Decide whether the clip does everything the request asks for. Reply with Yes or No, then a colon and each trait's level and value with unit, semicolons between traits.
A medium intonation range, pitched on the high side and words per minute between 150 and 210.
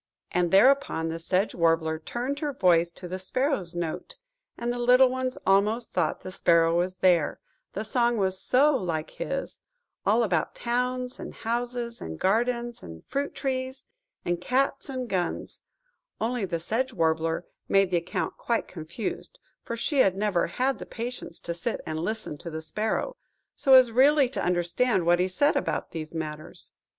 No: wide, 6.6 semitones; high, 210 Hz; average, 165 wpm